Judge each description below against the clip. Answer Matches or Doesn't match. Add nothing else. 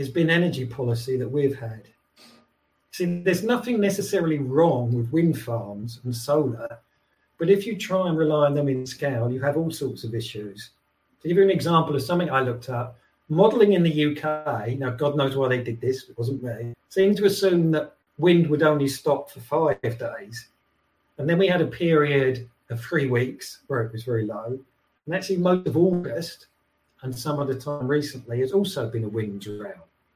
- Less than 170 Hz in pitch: Matches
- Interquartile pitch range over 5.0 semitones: Matches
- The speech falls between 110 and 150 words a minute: Doesn't match